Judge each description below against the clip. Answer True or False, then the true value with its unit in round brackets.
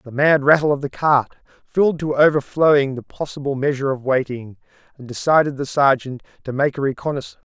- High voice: False (140 Hz)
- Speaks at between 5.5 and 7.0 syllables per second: True (6.1 syllables/s)